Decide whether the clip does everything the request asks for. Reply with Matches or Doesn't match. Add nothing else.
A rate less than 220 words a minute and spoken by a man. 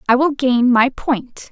Doesn't match